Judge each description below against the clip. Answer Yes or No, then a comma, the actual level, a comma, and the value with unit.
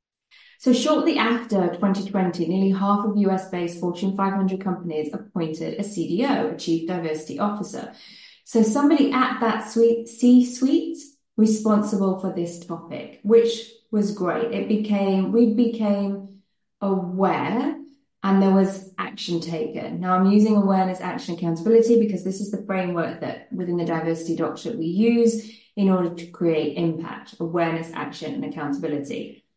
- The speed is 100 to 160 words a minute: Yes, average, 140 wpm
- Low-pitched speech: No, high, 195 Hz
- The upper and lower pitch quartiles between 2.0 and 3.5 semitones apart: No, average, 4.6 semitones